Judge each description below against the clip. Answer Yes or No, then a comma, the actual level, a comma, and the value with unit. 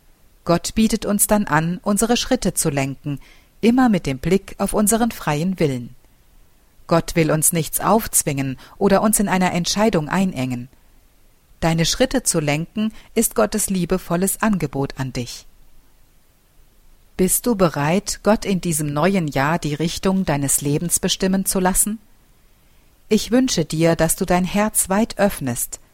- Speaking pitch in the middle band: Yes, medium, 180 Hz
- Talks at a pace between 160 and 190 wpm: No, average, 145 wpm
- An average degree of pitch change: No, wide, 5.7 semitones